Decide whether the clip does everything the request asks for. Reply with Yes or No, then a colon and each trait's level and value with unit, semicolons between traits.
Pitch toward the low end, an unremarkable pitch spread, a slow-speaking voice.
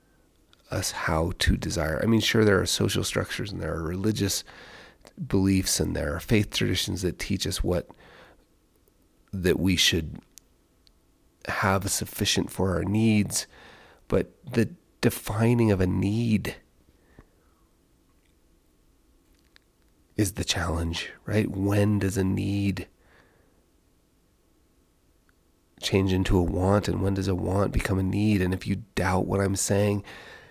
Yes: very low, 95 Hz; average, 3.0 semitones; slow, 130 wpm